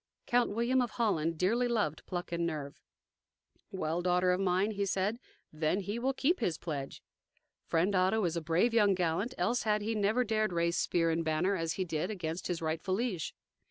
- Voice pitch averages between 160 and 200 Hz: Yes, medium, 185 Hz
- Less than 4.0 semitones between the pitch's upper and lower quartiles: No, average, 4.6 semitones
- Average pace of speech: Yes, average, 190 wpm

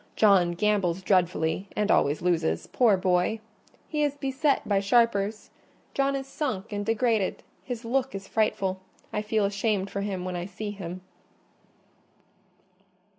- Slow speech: Yes, slow, 125 wpm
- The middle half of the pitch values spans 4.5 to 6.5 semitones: No, average, 3.5 semitones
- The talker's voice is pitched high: Yes, high, 205 Hz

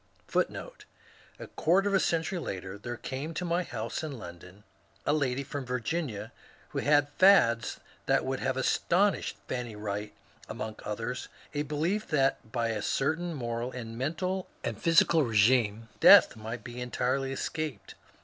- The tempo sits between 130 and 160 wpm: Yes, average, 155 wpm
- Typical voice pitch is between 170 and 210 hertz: No, low, 130 Hz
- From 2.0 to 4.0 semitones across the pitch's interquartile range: No, wide, 5.6 semitones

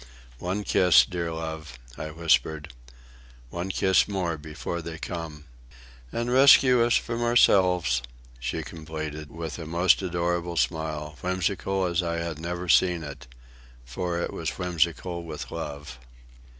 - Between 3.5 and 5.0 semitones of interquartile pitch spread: No, narrow, 2.5 semitones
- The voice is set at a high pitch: No, very low, 85 Hz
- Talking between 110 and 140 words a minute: Yes, slow, 135 wpm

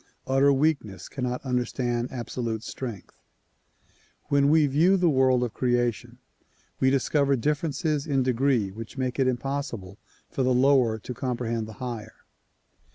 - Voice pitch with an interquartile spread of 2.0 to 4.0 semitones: Yes, average, 2.8 semitones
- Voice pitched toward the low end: Yes, low, 130 Hz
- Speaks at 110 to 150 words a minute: Yes, average, 140 wpm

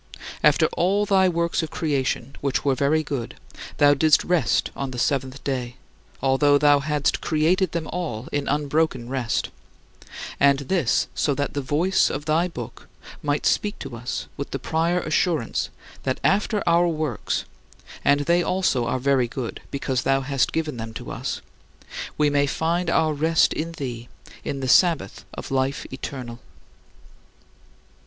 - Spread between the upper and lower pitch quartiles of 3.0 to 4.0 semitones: Yes, average, 3.6 semitones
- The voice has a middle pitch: Yes, medium, 145 Hz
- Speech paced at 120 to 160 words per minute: Yes, average, 155 wpm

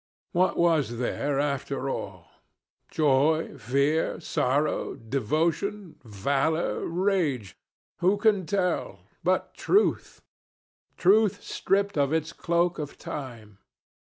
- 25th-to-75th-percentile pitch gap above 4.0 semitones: Yes, average, 4.9 semitones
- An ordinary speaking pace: No, slow, 100 wpm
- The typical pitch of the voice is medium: Yes, medium, 155 Hz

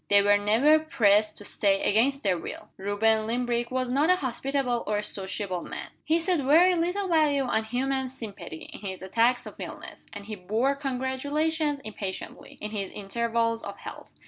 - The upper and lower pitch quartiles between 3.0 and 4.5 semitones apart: No, average, 5.3 semitones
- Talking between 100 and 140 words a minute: No, average, 175 wpm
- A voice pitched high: Yes, high, 235 Hz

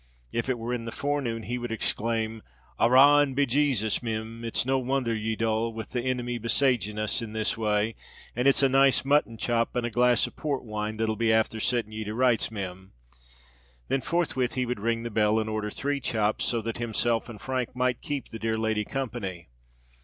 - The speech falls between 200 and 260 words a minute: Yes, fast, 205 wpm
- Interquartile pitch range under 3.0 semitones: Yes, narrow, 2.5 semitones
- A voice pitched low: Yes, low, 115 Hz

